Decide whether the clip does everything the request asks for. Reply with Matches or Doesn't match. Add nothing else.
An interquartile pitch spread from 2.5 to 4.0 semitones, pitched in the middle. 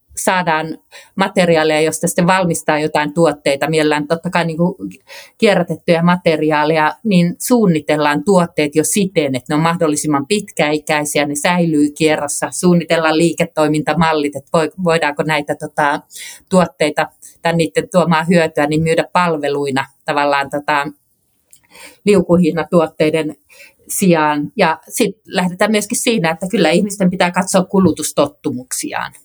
Matches